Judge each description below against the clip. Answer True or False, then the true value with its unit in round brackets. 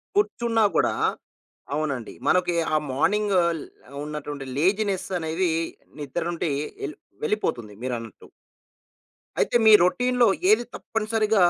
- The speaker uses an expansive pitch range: True (6.5 semitones)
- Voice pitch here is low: False (180 Hz)